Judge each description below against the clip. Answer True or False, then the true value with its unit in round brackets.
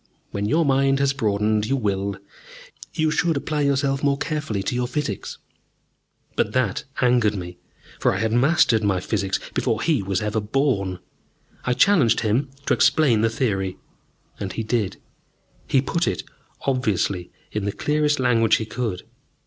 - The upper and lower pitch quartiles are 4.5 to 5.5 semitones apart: True (5.2 semitones)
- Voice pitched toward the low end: True (115 Hz)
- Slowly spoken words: False (155 wpm)